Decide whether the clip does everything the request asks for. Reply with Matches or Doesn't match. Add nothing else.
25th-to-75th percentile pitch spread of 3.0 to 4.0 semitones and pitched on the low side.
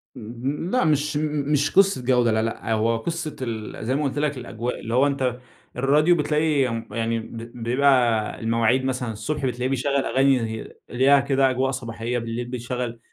Matches